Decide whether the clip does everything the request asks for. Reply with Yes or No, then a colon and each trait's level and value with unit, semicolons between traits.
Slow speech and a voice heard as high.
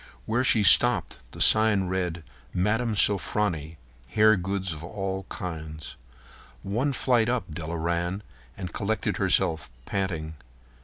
No: slow, 120 wpm; very low, 95 Hz